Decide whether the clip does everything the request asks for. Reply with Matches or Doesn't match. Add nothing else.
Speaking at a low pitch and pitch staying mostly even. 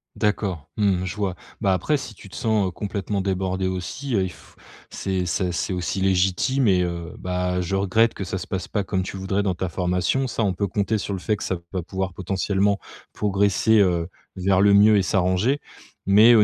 Matches